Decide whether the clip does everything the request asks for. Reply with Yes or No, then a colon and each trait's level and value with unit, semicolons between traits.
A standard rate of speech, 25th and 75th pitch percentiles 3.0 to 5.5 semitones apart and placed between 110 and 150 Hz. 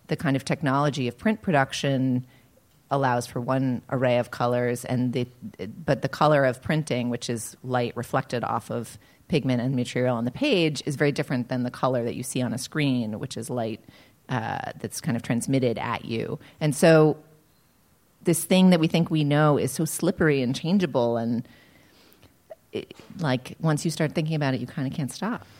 Yes: average, 190 wpm; average, 4.0 semitones; low, 135 Hz